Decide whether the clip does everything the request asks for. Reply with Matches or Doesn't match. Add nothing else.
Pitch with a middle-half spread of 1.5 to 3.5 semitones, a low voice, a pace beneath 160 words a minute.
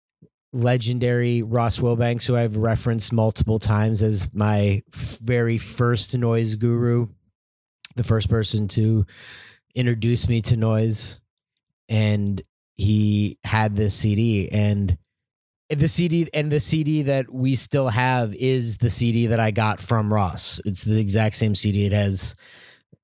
Matches